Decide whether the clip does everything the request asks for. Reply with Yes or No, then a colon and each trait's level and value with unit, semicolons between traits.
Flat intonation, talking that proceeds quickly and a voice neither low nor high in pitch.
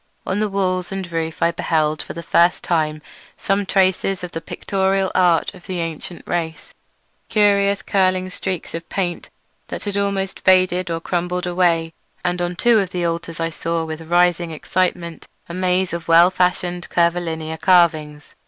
No: narrow, 2.1 semitones; average, 165 wpm; medium, 175 Hz